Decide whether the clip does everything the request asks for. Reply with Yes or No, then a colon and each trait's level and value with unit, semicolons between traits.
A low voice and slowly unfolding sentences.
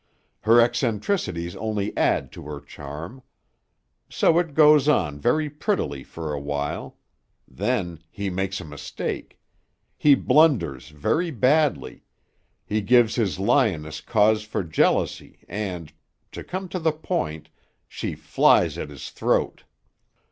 Yes: low, 105 Hz; slow, 125 wpm